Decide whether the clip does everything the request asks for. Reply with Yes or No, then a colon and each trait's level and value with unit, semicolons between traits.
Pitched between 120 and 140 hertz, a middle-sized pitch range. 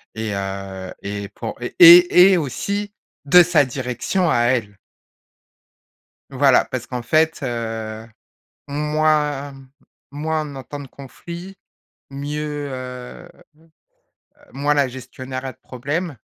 Yes: low, 135 Hz; average, 3.7 semitones